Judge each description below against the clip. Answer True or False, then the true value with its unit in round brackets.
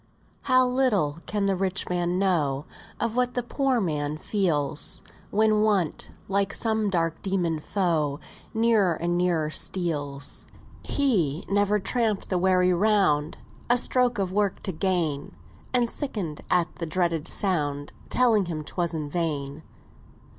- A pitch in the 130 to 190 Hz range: True (185 Hz)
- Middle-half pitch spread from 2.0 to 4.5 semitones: False (5.1 semitones)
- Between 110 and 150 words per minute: True (140 wpm)